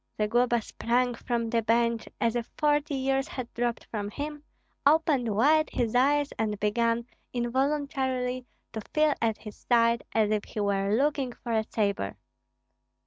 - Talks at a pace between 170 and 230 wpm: No, average, 150 wpm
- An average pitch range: Yes, average, 3.3 semitones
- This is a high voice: Yes, high, 240 Hz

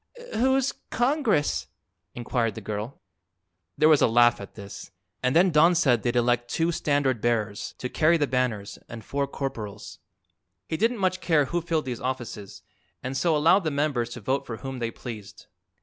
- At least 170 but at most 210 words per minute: Yes, average, 175 wpm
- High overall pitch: No, low, 130 Hz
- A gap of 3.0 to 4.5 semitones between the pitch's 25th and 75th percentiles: No, wide, 5.5 semitones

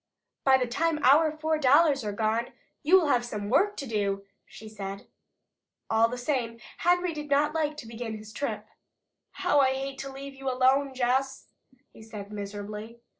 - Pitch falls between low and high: No, very high, 260 Hz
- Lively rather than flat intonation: No, average, 4.7 semitones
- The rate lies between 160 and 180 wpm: Yes, average, 175 wpm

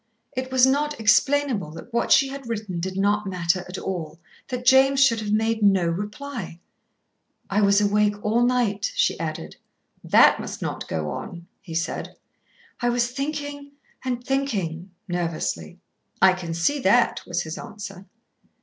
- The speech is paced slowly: No, average, 155 wpm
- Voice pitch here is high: Yes, high, 210 Hz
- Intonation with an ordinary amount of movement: No, wide, 6.1 semitones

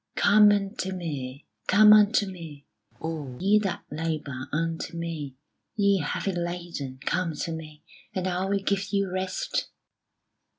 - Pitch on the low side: No, medium, 175 Hz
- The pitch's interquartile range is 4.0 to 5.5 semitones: Yes, average, 4.3 semitones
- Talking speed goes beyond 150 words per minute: No, slow, 135 wpm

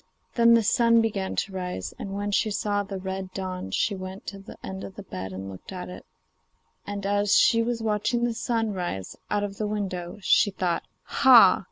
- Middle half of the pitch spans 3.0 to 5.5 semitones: No, narrow, 2.5 semitones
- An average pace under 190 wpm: No, fast, 205 wpm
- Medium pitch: No, high, 200 Hz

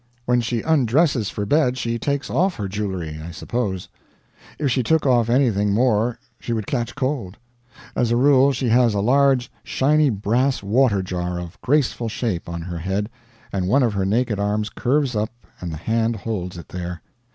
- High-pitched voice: No, low, 115 Hz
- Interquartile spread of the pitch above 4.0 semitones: Yes, average, 4.7 semitones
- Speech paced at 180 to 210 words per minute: Yes, average, 185 wpm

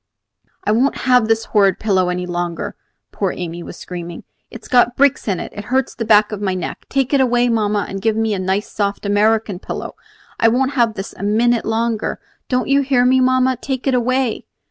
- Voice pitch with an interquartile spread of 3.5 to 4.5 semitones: Yes, average, 4.0 semitones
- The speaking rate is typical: No, fast, 210 wpm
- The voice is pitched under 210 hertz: No, high, 225 Hz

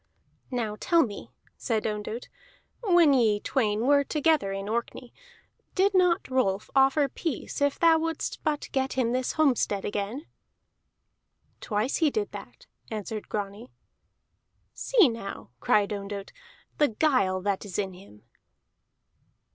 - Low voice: No, high, 245 Hz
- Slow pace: Yes, slow, 130 wpm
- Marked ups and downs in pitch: Yes, wide, 6.3 semitones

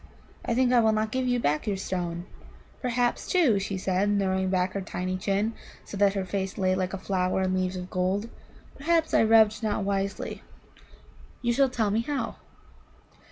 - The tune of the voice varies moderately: Yes, average, 3.4 semitones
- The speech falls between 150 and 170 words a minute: No, average, 185 wpm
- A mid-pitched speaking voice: No, high, 200 Hz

